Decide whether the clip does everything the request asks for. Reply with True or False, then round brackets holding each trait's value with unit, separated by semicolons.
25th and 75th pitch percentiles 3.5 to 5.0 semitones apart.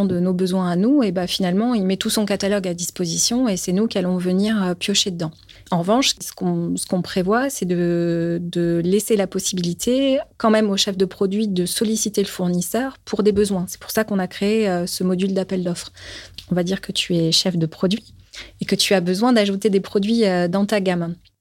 False (2.9 semitones)